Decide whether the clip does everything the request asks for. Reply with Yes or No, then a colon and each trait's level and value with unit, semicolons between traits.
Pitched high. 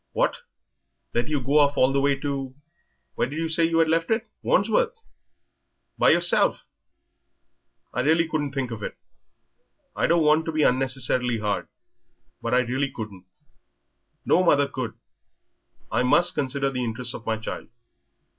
No: medium, 140 Hz